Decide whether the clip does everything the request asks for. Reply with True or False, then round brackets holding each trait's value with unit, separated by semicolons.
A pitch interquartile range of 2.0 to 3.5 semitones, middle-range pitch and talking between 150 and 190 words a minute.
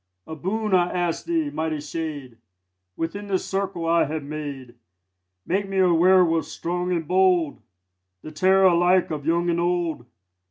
True (2.9 semitones; 170 Hz; 155 wpm)